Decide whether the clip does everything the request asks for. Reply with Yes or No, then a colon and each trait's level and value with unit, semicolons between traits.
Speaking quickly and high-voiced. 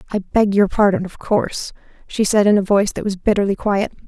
Yes: fast, 220 wpm; high, 200 Hz